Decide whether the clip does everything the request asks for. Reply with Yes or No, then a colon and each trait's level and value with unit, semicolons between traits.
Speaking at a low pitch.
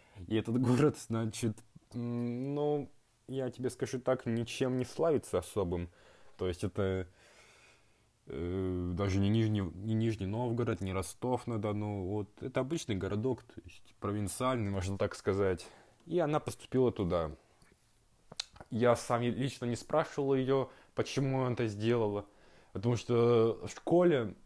Yes: low, 115 Hz